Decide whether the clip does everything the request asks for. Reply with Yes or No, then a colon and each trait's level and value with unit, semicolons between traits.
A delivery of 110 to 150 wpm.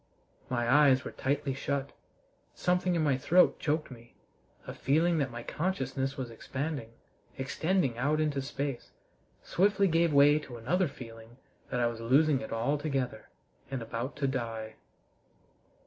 Yes: average, 145 wpm